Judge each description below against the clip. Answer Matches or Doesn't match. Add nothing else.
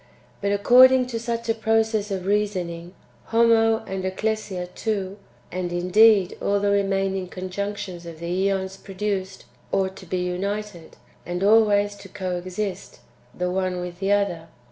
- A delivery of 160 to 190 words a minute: Doesn't match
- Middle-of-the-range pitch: Doesn't match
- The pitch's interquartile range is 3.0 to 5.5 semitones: Doesn't match